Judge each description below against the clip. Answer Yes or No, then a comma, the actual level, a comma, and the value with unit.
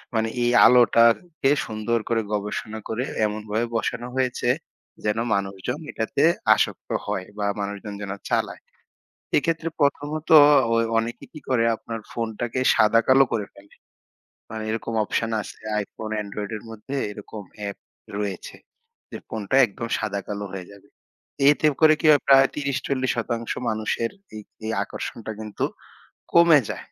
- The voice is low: Yes, low, 115 Hz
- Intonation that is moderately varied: Yes, average, 3.5 semitones